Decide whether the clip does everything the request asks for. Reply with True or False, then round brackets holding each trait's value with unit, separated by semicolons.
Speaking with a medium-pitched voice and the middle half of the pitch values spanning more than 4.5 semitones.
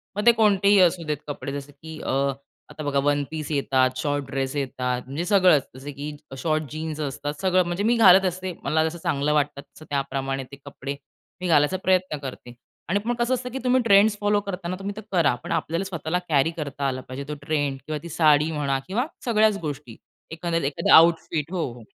True (155 Hz; 4.9 semitones)